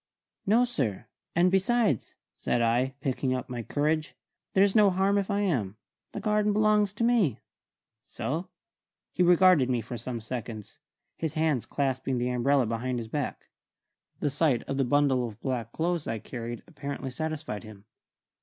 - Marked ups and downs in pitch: Yes, wide, 7.0 semitones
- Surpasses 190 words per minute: No, average, 160 wpm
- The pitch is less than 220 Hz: Yes, medium, 140 Hz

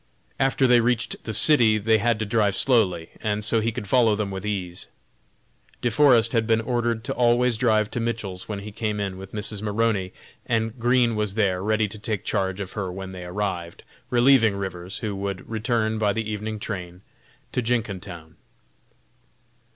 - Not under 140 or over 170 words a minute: No, average, 180 wpm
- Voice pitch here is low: Yes, low, 110 Hz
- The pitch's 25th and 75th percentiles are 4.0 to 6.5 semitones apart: No, average, 2.8 semitones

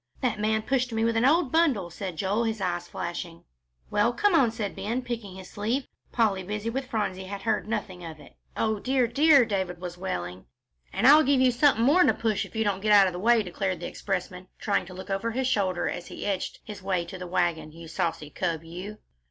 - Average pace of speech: No, fast, 225 wpm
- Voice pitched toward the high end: Yes, high, 205 Hz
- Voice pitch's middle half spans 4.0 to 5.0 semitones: Yes, average, 4.3 semitones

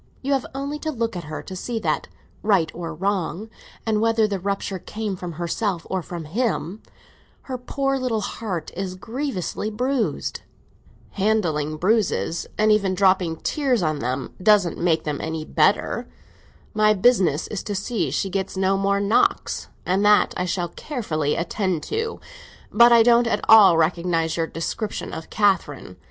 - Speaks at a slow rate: No, average, 155 wpm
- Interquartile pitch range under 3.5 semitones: No, average, 4.6 semitones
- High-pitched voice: Yes, high, 195 Hz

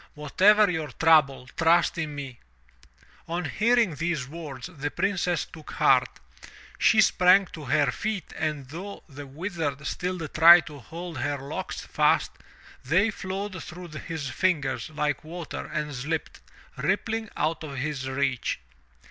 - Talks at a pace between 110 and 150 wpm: Yes, average, 140 wpm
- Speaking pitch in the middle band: Yes, medium, 160 Hz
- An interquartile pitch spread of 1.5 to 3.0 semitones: No, average, 4.0 semitones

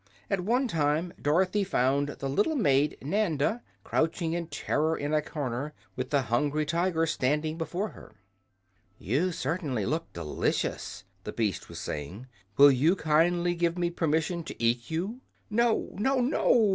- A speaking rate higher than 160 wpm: No, average, 150 wpm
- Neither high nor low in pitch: Yes, medium, 160 Hz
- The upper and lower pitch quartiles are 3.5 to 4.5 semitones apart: Yes, average, 4.2 semitones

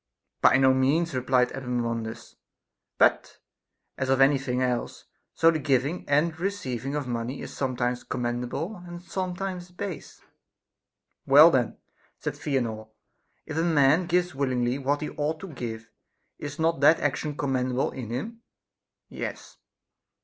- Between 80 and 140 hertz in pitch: Yes, low, 135 Hz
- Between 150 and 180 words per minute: No, average, 140 wpm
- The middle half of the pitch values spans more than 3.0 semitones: Yes, average, 4.6 semitones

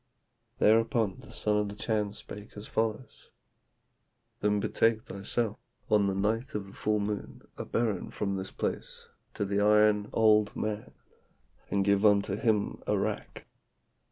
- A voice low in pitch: Yes, low, 105 Hz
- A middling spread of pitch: No, narrow, 1.3 semitones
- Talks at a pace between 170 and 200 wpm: No, average, 145 wpm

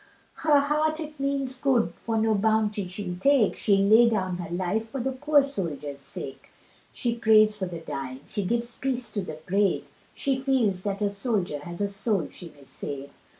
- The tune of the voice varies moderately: No, wide, 6.1 semitones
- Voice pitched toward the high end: Yes, high, 210 Hz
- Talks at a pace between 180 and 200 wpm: Yes, average, 190 wpm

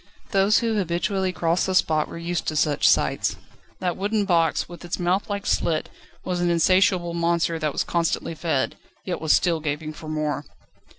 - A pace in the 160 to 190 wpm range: Yes, average, 180 wpm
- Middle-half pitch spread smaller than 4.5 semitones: Yes, narrow, 2.5 semitones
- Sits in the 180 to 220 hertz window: No, medium, 170 Hz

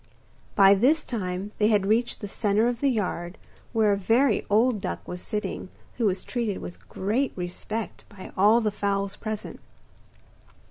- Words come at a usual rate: Yes, average, 160 wpm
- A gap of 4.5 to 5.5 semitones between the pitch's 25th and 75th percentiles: No, average, 2.7 semitones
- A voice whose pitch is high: Yes, high, 210 Hz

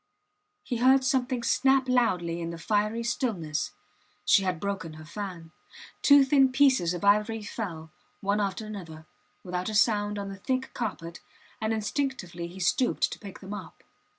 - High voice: Yes, high, 205 Hz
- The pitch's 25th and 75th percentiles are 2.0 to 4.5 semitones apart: No, wide, 5.5 semitones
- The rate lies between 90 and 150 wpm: No, average, 160 wpm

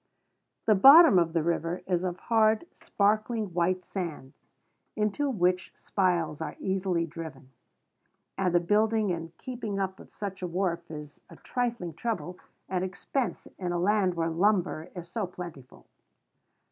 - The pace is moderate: Yes, average, 145 wpm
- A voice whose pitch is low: No, medium, 180 Hz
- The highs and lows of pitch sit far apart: No, average, 3.7 semitones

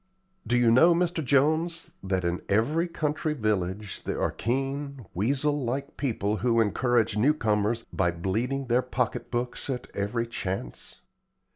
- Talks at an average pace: Yes, average, 145 wpm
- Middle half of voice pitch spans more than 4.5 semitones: Yes, average, 5.0 semitones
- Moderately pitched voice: No, low, 120 Hz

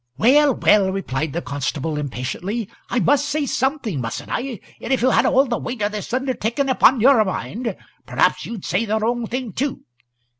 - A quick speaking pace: No, average, 185 wpm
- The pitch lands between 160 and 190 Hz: No, high, 230 Hz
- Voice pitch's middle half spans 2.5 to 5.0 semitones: No, wide, 5.4 semitones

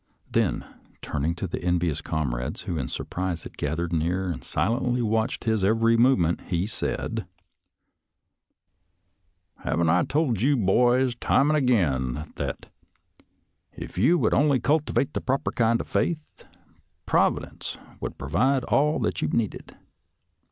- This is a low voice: Yes, low, 105 Hz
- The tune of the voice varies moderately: No, wide, 7.1 semitones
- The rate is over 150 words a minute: No, slow, 135 wpm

